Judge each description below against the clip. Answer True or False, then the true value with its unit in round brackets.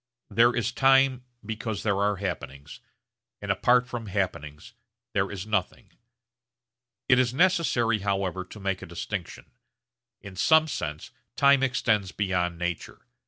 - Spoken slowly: True (130 wpm)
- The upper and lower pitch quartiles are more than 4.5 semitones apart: True (5.0 semitones)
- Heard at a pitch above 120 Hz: False (105 Hz)